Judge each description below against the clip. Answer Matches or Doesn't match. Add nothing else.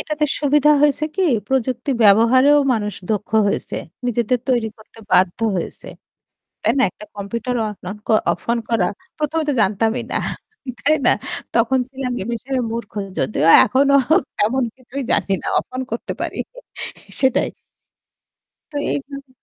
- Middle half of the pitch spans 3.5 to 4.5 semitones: Matches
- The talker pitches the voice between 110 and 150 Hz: Doesn't match